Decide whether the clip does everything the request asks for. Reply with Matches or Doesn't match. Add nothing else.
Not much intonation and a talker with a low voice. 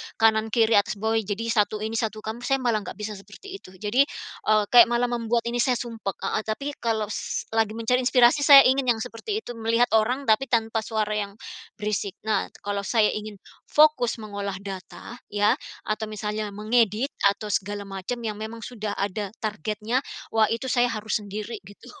Doesn't match